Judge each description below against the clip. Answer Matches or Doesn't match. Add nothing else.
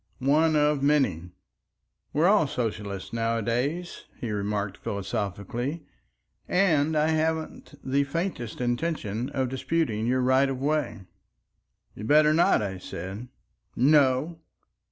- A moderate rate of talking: Doesn't match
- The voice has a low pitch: Matches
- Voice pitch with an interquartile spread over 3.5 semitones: Matches